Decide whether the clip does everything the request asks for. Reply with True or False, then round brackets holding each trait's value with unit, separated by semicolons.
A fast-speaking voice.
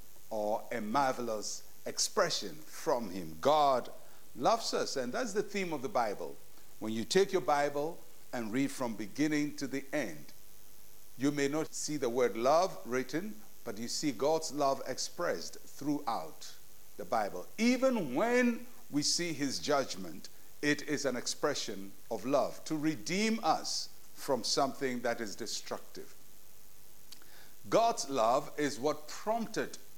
False (140 wpm)